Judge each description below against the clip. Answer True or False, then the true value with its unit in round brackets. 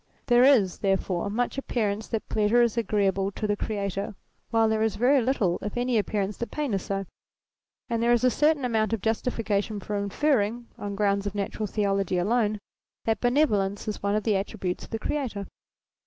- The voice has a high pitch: True (215 Hz)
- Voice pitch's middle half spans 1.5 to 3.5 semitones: True (3.0 semitones)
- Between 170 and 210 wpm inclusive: True (190 wpm)